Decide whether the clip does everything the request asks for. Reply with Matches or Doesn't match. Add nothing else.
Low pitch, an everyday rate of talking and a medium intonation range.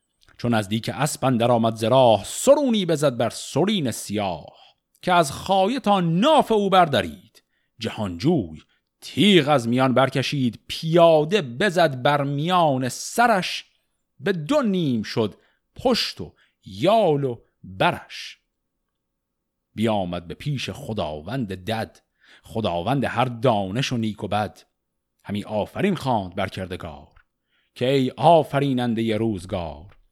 Doesn't match